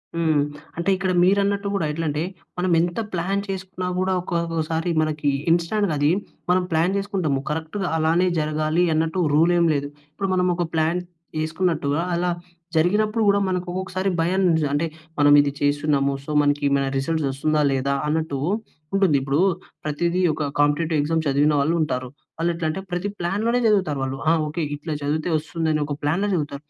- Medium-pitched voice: Yes, medium, 165 Hz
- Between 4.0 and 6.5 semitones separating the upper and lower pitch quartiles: No, average, 3.4 semitones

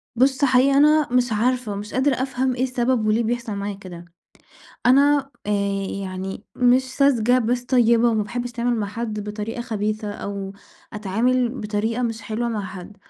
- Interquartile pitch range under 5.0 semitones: Yes, average, 3.2 semitones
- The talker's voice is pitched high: Yes, high, 235 Hz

